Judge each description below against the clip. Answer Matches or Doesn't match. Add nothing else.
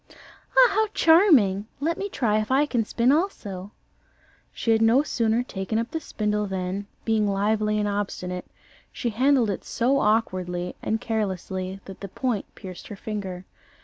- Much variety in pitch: Doesn't match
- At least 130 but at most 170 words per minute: Matches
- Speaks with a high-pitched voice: Matches